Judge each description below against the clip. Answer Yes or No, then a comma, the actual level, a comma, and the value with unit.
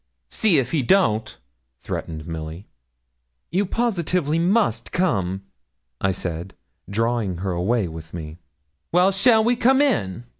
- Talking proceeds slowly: Yes, slow, 125 wpm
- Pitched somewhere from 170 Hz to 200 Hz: No, low, 115 Hz